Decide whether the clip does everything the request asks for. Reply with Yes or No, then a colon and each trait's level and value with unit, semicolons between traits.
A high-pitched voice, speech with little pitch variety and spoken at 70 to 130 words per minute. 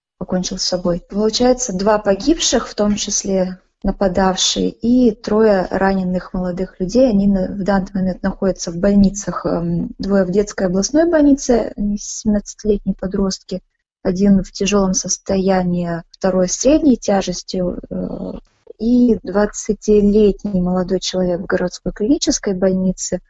Yes: high, 195 Hz; narrow, 2.3 semitones; average, 115 wpm